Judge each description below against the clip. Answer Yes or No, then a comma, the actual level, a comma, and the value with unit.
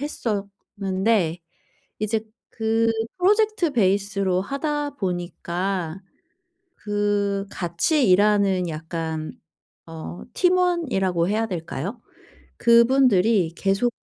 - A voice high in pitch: Yes, high, 200 Hz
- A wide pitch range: No, average, 4.5 semitones